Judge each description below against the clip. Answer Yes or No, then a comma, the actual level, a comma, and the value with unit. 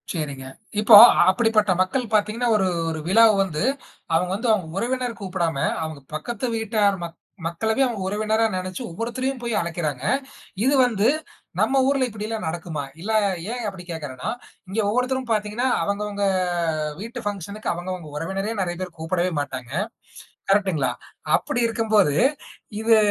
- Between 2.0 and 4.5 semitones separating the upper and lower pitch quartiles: No, average, 4.9 semitones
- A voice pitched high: Yes, high, 205 Hz